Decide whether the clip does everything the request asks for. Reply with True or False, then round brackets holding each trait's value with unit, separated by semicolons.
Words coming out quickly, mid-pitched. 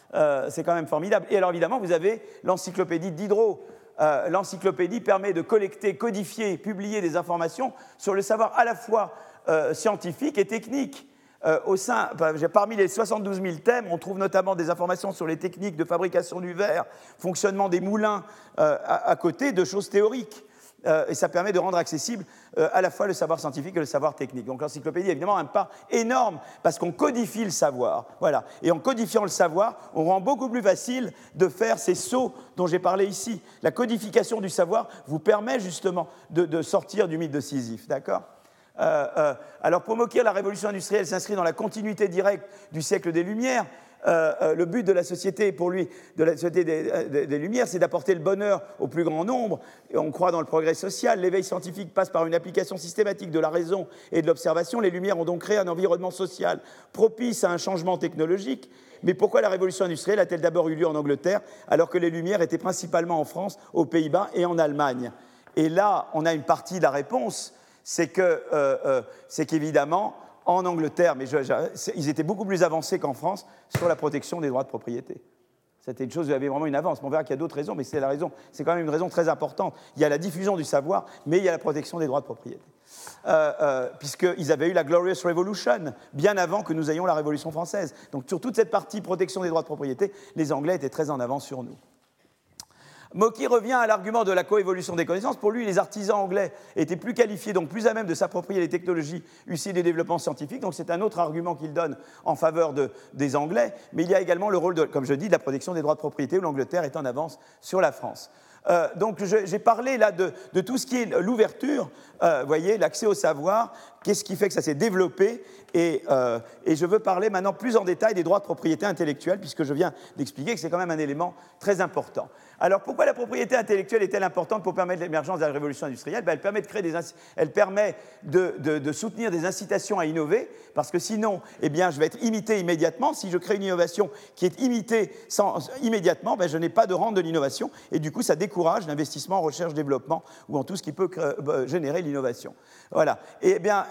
True (225 wpm; 180 Hz)